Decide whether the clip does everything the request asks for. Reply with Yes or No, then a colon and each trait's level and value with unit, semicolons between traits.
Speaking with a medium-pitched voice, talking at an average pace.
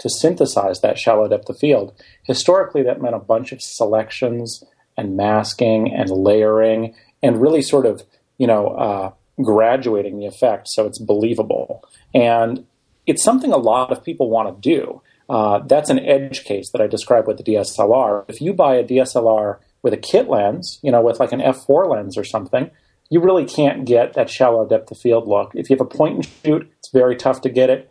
No: low, 115 Hz; average, 195 wpm